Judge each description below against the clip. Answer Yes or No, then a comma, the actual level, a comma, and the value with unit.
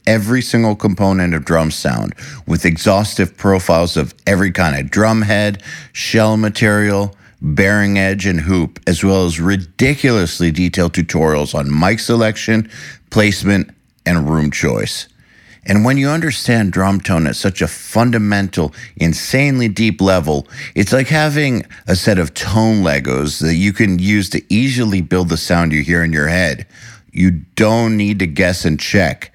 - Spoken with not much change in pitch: No, average, 4.3 semitones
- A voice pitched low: Yes, very low, 95 Hz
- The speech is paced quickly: No, average, 155 wpm